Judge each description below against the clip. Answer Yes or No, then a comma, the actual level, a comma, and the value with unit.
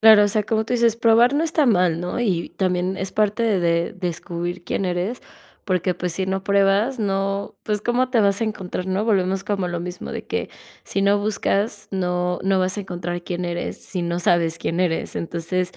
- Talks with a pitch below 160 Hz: No, high, 190 Hz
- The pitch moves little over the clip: No, average, 3.0 semitones